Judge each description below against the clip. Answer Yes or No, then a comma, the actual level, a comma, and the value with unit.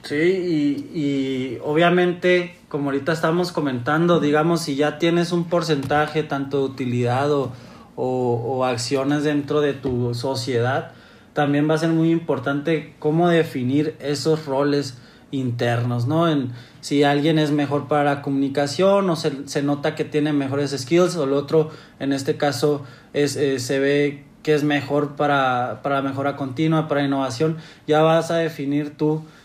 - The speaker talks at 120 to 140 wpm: No, average, 155 wpm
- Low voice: No, medium, 145 Hz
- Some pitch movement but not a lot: No, narrow, 2.2 semitones